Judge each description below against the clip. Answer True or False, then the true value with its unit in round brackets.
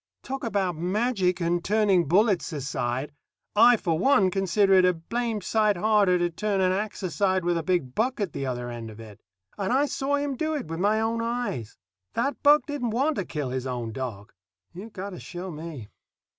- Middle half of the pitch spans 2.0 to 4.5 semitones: False (5.4 semitones)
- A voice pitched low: False (190 Hz)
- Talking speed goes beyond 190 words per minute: True (200 wpm)